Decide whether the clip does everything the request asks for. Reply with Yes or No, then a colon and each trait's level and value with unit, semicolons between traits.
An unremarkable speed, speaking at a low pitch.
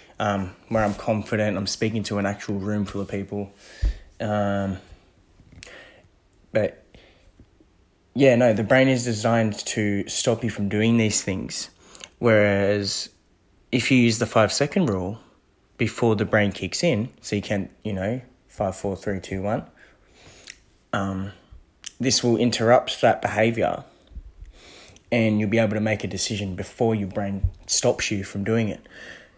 Yes: average, 150 wpm; low, 105 Hz